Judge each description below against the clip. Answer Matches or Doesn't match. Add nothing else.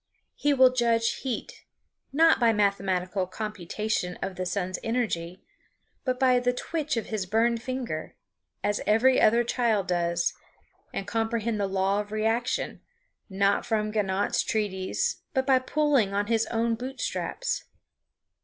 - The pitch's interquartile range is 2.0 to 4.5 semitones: Matches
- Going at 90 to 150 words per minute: Matches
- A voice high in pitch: Matches